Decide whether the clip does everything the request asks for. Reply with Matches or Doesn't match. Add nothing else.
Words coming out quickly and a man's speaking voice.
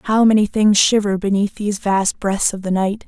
Doesn't match